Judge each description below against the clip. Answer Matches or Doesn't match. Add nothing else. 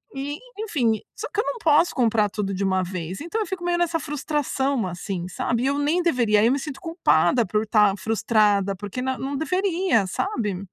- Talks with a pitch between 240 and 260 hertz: Matches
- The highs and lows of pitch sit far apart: Matches